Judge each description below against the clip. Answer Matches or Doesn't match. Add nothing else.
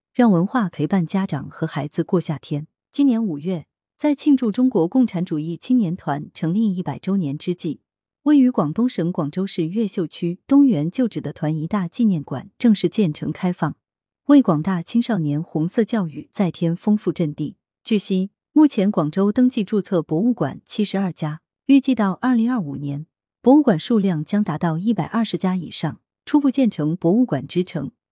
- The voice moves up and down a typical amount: Doesn't match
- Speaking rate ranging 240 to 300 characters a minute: Matches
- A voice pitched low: Doesn't match